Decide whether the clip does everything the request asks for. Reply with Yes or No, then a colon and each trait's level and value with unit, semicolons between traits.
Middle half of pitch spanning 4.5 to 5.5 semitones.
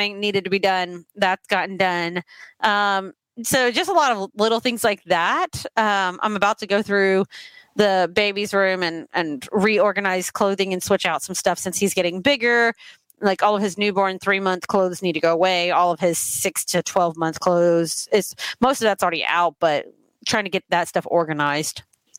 No: average, 3.0 semitones